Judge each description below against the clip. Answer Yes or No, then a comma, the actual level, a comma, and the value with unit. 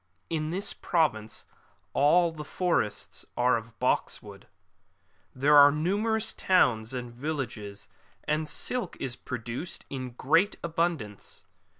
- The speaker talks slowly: Yes, slow, 125 wpm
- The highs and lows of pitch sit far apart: Yes, wide, 5.9 semitones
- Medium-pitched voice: Yes, medium, 145 Hz